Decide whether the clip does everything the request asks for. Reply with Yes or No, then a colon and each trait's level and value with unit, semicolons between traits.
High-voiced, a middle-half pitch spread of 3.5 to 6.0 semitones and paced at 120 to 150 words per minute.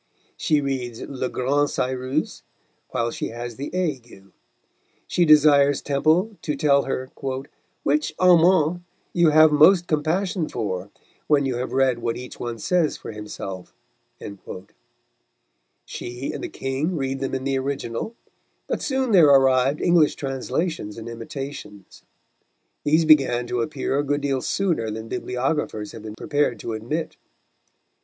No: medium, 140 Hz; average, 4.2 semitones; average, 140 wpm